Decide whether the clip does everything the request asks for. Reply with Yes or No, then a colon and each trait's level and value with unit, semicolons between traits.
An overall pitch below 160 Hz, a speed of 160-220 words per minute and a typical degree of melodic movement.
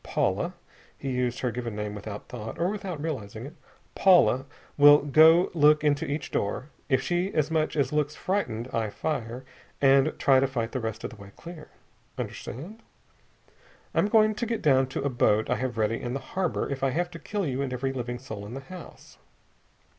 Yes: low, 135 Hz; average, 200 wpm; average, 4.8 semitones